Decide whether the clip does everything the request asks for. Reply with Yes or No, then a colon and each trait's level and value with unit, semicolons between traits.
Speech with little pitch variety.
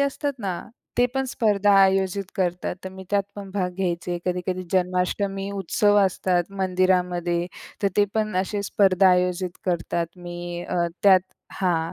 Yes: narrow, 1.9 semitones